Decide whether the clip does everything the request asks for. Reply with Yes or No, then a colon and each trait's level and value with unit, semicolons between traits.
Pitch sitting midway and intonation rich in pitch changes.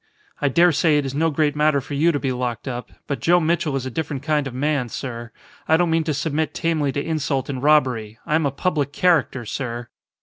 No: medium, 145 Hz; average, 3.3 semitones